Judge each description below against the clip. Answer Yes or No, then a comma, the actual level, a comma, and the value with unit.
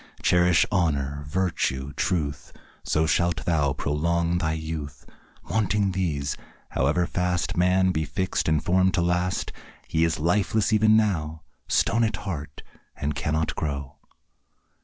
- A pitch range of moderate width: Yes, average, 3.6 semitones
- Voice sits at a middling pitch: No, very low, 85 Hz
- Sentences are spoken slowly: Yes, slow, 130 wpm